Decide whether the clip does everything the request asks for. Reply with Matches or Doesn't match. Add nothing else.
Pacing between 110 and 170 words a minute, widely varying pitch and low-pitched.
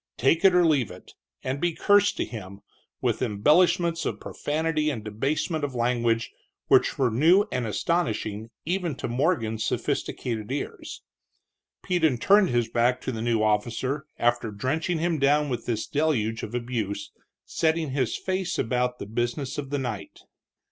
Matches